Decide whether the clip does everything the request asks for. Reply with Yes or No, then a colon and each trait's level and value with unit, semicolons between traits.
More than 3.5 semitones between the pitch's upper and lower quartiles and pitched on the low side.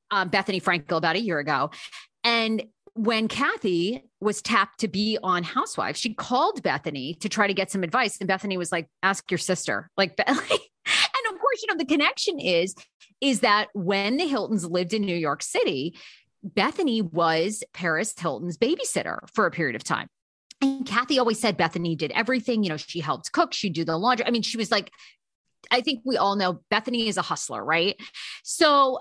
No: wide, 5.6 semitones; high, 215 Hz